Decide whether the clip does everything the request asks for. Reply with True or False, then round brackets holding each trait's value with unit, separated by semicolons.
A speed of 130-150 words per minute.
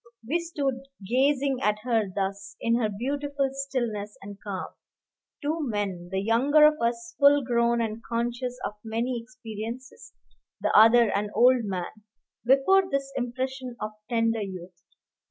True (140 wpm)